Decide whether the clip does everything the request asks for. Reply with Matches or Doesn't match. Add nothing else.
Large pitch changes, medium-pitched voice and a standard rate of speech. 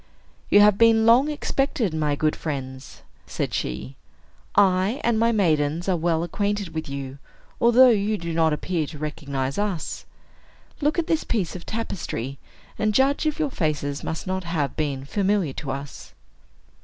Matches